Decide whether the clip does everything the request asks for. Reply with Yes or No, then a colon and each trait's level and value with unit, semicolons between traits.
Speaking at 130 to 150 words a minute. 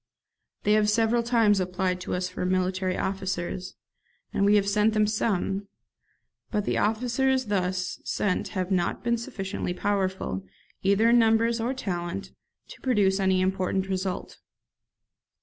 Yes: average, 140 wpm